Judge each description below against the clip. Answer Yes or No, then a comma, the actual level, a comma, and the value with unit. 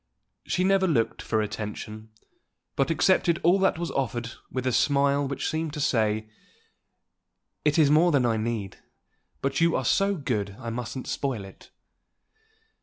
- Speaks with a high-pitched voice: No, low, 135 Hz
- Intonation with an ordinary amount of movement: No, wide, 6.1 semitones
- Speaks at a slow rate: No, average, 155 wpm